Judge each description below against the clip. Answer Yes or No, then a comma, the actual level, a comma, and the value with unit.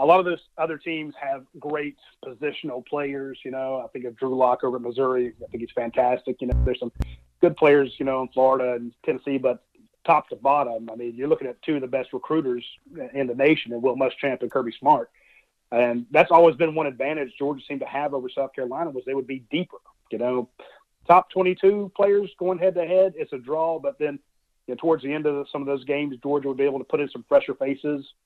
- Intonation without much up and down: No, average, 3.8 semitones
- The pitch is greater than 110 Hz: Yes, medium, 140 Hz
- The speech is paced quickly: Yes, fast, 235 wpm